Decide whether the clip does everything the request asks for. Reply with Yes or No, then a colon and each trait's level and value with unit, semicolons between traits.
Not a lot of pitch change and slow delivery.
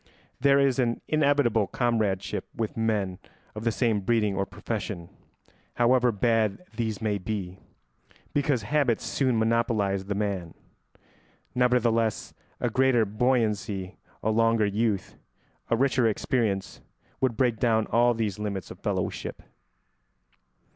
No: average, 3.0 semitones; slow, 120 wpm